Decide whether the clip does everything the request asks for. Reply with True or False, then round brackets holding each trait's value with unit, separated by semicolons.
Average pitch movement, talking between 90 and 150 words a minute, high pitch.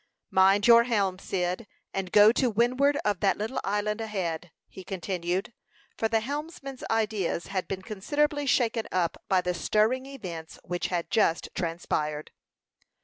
True (4.5 semitones; 145 wpm; 205 Hz)